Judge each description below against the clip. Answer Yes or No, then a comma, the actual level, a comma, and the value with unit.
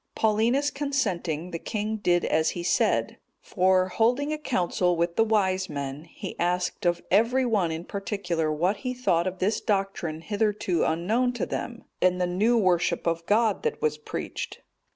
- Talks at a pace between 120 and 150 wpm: No, average, 170 wpm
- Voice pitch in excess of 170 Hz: Yes, medium, 185 Hz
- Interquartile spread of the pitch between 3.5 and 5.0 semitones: Yes, average, 4.4 semitones